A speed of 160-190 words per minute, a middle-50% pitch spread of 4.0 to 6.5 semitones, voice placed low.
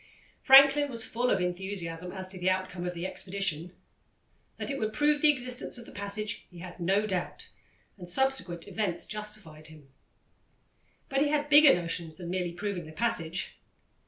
No: average, 170 wpm; average, 5.2 semitones; high, 190 Hz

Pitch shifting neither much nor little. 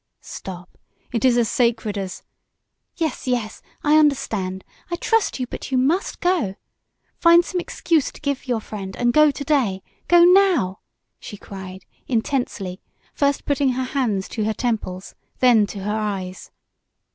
No: wide, 6.6 semitones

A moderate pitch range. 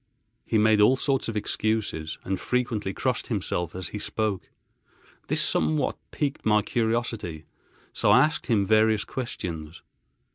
Yes: average, 3.7 semitones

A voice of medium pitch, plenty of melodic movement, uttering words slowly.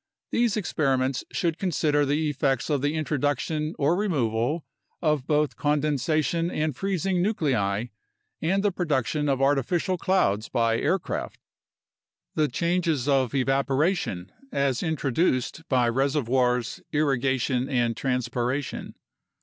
No: medium, 145 Hz; average, 3.9 semitones; slow, 110 wpm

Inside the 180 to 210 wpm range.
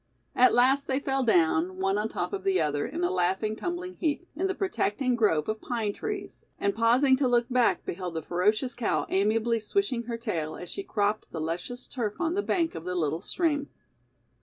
Yes: fast, 205 wpm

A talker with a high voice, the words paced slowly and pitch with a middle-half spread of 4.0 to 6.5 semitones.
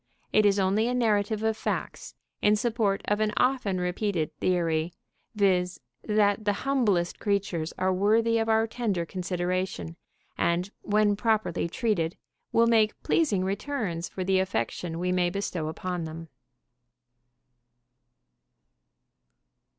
No: high, 200 Hz; slow, 125 wpm; average, 3.4 semitones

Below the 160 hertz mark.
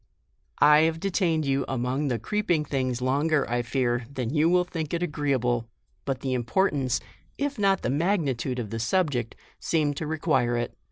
Yes: medium, 140 Hz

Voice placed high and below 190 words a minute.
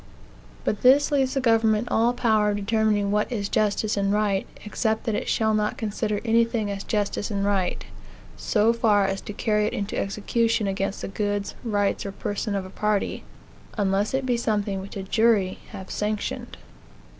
Yes: high, 210 Hz; average, 180 wpm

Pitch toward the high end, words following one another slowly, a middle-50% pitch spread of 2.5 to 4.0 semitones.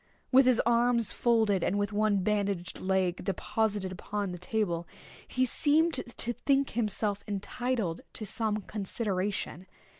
Yes: high, 210 Hz; slow, 130 wpm; average, 3.6 semitones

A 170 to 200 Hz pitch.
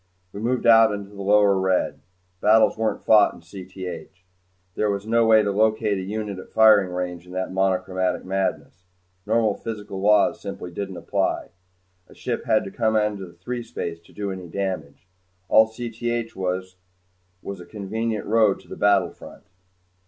No: low, 100 Hz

